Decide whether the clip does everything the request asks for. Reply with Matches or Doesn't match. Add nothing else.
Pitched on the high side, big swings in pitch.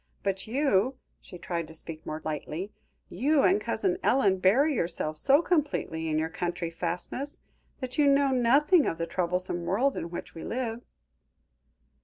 Matches